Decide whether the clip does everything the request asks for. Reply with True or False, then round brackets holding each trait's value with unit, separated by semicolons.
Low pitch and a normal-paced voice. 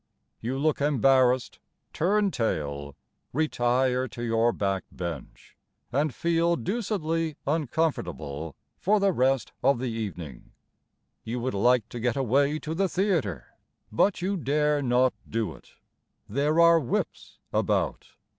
False (130 Hz; 125 wpm)